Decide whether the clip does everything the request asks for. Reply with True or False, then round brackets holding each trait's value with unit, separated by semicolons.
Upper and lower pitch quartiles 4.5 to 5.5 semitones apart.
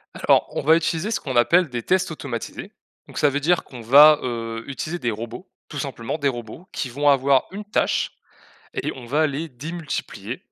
True (5.1 semitones)